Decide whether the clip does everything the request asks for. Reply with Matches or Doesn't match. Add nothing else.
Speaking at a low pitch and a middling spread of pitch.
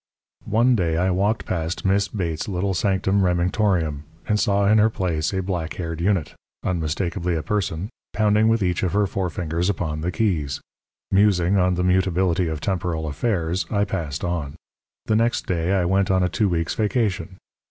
Matches